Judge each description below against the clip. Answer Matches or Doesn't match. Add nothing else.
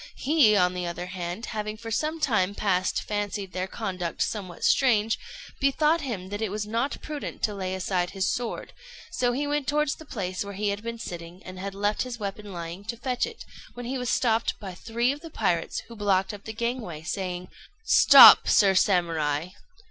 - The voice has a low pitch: Doesn't match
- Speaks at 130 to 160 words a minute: Doesn't match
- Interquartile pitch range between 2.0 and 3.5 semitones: Doesn't match